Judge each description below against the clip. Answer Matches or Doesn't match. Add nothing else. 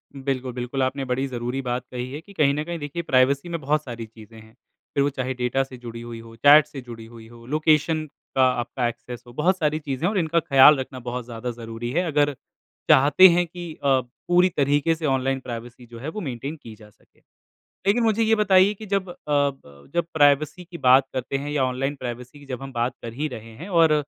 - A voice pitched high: Doesn't match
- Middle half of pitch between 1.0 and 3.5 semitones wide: Doesn't match